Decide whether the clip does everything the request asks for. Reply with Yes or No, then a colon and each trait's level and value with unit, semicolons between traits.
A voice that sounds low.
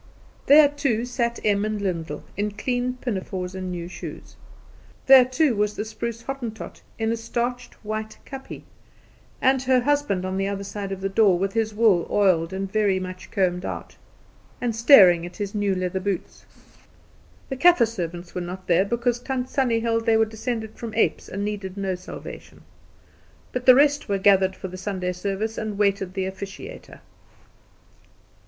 No: high, 210 Hz